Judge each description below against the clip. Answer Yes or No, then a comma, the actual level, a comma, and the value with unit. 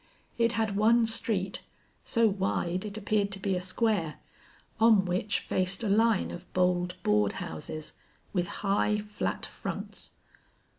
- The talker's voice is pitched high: Yes, high, 200 Hz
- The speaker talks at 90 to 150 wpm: Yes, average, 140 wpm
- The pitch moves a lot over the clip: No, average, 3.1 semitones